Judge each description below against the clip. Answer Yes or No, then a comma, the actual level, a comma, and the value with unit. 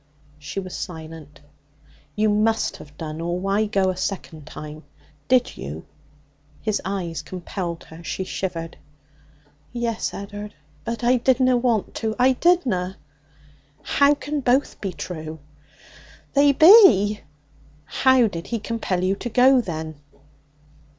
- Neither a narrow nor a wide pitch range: No, wide, 6.3 semitones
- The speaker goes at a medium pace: No, slow, 130 wpm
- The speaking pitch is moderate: No, high, 200 Hz